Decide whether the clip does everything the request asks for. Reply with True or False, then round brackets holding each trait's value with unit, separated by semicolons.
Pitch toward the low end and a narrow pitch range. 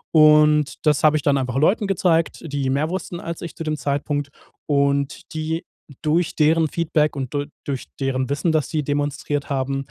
False (150 Hz; 2.1 semitones)